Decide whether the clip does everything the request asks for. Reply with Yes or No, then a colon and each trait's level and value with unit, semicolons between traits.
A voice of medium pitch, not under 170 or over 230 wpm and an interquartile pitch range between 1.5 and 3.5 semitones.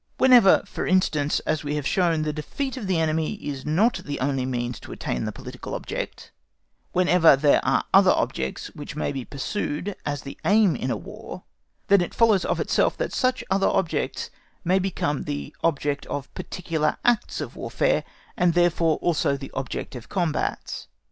No: medium, 160 Hz; average, 175 wpm; average, 5.0 semitones